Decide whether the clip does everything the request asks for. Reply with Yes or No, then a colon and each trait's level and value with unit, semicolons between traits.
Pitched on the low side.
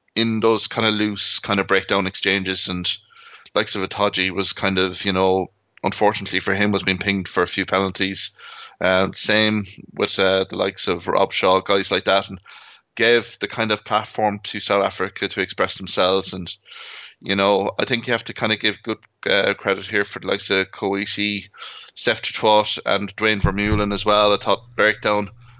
Yes: low, 100 Hz